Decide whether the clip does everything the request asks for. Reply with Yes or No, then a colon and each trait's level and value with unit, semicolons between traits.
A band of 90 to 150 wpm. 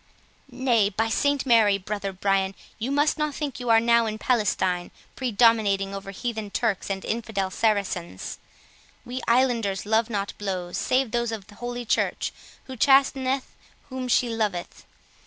Yes: average, 145 wpm